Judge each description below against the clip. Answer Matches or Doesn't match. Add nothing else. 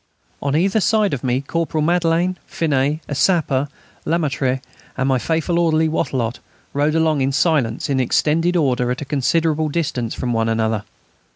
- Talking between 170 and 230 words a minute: Doesn't match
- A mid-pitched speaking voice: Matches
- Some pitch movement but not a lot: Matches